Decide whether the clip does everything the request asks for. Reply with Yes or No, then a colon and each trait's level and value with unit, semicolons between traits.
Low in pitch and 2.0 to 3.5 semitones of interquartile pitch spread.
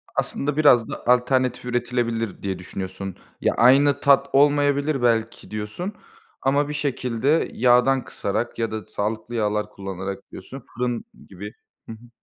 No: low, 120 Hz; average, 4.3 semitones